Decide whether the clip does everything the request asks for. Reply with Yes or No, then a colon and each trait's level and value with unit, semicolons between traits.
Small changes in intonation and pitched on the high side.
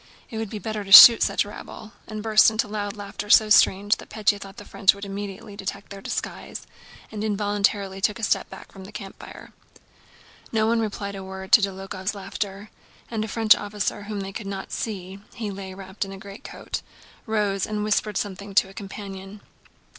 Yes: narrow, 1.5 semitones; high, 205 Hz